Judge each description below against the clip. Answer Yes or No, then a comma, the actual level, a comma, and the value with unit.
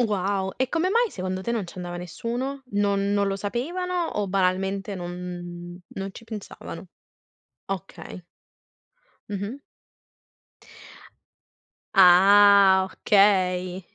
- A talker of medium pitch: No, high, 195 Hz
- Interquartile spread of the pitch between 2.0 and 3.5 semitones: Yes, narrow, 2.3 semitones